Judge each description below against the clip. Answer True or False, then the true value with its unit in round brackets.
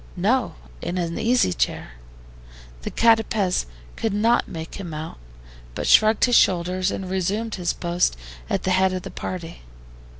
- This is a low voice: False (185 Hz)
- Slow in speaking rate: False (155 wpm)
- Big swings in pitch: False (3.8 semitones)